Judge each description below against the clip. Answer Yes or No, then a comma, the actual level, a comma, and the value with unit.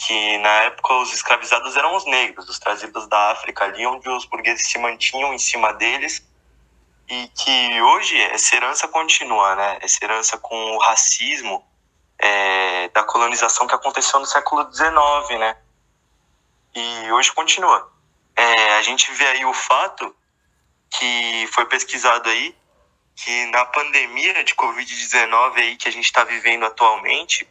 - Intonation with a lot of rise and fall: No, average, 3.6 semitones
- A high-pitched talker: No, low, 115 Hz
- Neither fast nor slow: Yes, average, 150 wpm